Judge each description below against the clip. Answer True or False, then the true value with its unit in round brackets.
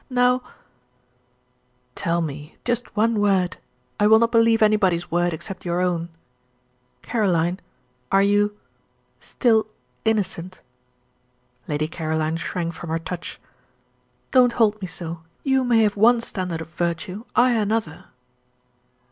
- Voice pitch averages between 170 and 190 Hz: True (185 Hz)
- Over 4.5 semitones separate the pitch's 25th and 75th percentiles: True (5.0 semitones)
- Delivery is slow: True (125 wpm)